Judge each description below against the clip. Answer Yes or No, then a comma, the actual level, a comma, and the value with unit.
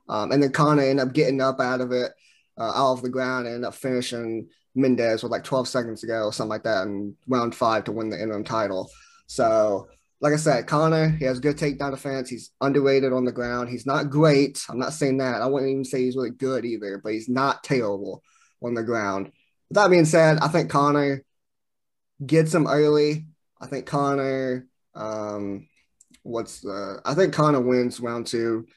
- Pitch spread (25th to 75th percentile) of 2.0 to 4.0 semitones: Yes, average, 3.5 semitones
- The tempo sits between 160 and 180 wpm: No, fast, 205 wpm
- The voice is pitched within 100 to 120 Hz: No, low, 130 Hz